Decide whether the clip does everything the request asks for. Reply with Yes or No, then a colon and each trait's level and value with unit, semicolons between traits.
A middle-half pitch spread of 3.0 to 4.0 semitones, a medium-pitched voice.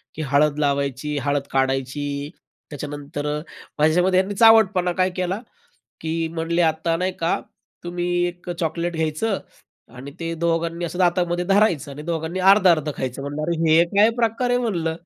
Yes: average, 3.5 semitones; medium, 165 Hz